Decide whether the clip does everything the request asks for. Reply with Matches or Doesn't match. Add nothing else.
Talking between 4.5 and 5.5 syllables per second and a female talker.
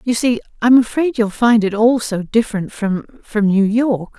Matches